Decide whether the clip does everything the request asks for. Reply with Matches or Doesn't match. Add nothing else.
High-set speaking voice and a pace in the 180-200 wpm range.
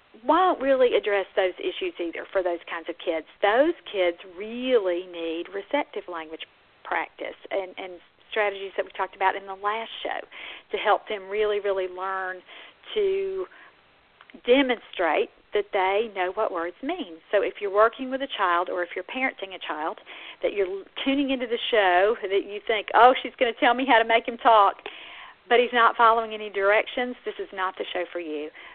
Matches